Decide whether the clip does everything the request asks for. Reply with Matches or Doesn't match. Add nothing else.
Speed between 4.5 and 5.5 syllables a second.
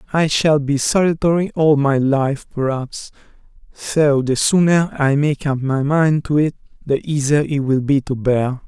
Doesn't match